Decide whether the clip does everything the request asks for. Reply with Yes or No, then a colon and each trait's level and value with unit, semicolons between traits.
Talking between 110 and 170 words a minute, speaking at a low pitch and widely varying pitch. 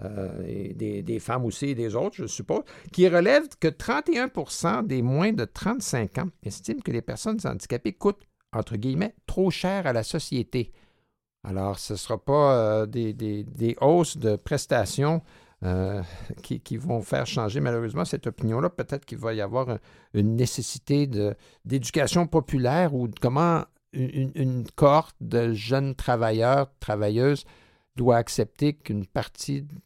Yes: average, 160 wpm; low, 130 Hz; wide, 6.1 semitones